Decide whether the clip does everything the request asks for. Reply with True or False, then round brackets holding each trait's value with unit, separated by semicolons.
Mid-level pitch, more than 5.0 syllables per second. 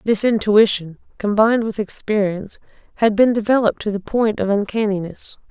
False (210 Hz; 5.5 syllables/s)